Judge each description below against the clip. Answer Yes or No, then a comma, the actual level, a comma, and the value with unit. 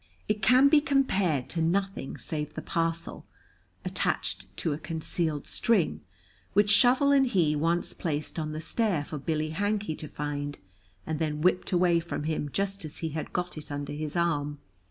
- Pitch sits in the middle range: Yes, medium, 165 Hz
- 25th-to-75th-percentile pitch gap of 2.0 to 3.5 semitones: No, average, 4.4 semitones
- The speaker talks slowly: No, average, 175 wpm